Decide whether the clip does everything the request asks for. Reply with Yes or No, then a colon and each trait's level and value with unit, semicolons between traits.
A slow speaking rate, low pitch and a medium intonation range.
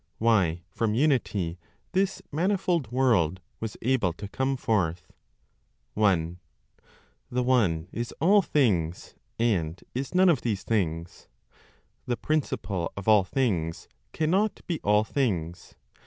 No: slow, 120 wpm; low, 110 Hz; wide, 7.2 semitones